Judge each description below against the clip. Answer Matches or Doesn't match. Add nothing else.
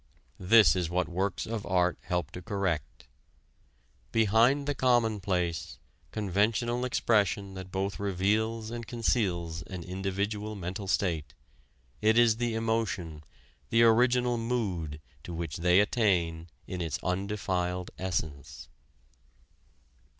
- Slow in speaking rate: Matches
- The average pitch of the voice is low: Matches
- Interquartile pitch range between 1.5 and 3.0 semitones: Doesn't match